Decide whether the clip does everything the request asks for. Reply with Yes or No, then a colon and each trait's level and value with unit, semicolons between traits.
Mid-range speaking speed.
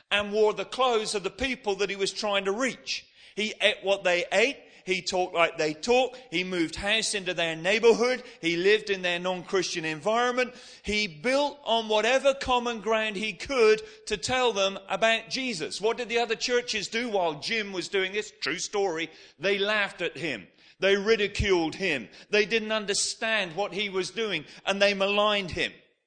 Yes: average, 180 wpm